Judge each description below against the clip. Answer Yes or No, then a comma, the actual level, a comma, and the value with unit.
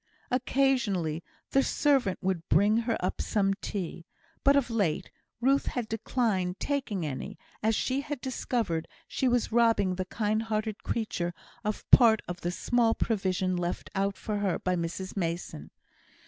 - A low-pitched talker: No, high, 210 Hz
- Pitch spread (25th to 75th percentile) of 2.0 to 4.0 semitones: No, average, 4.7 semitones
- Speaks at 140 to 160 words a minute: Yes, average, 150 wpm